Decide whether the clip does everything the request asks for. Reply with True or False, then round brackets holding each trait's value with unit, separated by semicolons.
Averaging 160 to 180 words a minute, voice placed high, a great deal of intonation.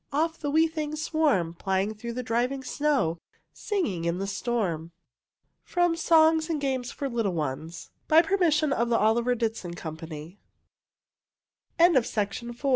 False (145 wpm; 240 Hz; 8.3 semitones)